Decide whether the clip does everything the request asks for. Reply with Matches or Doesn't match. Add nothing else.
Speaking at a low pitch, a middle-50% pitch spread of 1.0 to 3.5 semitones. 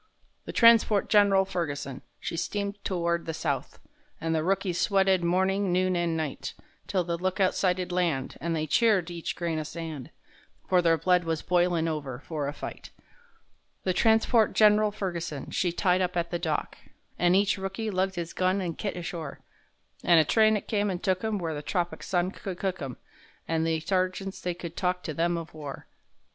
Doesn't match